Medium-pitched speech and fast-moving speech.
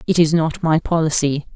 No: medium, 160 Hz; average, 195 wpm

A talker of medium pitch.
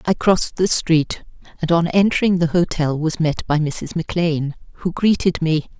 Yes: medium, 165 Hz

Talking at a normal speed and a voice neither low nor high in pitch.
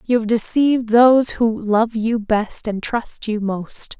No: average, 180 wpm; high, 225 Hz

